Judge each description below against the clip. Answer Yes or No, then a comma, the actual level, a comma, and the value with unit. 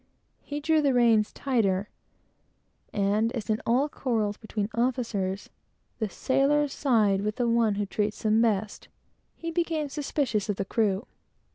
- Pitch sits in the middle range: No, high, 225 Hz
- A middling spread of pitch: Yes, average, 4.6 semitones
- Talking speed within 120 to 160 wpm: Yes, average, 145 wpm